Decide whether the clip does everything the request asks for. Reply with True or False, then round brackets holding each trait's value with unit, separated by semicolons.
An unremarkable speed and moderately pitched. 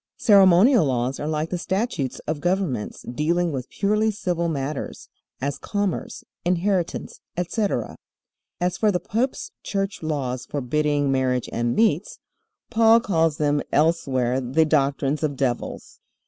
False (130 wpm; 160 Hz)